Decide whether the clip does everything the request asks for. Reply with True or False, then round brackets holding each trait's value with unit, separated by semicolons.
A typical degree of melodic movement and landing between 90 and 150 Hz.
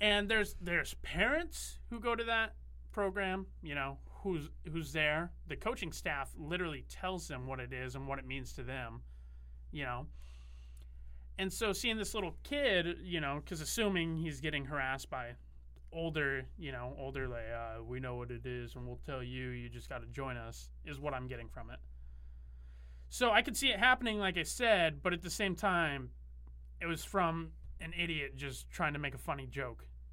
False (6.9 semitones; 140 Hz)